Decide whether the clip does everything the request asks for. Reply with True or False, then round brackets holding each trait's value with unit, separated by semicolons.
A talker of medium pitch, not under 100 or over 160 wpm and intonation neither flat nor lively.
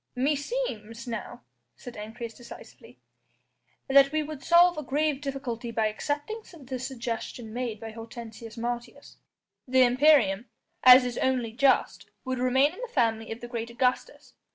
False (250 Hz; 145 wpm; 3.2 semitones)